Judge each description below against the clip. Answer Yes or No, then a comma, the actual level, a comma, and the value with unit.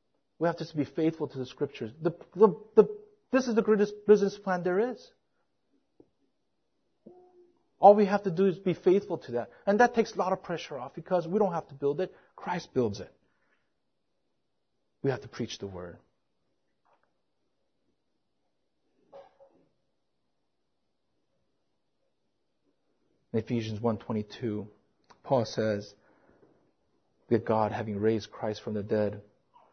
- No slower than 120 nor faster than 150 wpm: Yes, slow, 135 wpm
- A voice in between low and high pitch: Yes, medium, 160 Hz